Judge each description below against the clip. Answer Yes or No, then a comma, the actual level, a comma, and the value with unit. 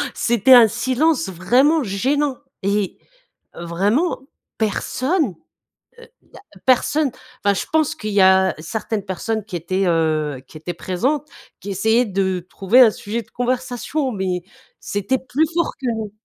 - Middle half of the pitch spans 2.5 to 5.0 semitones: No, wide, 5.5 semitones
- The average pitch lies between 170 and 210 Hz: No, high, 220 Hz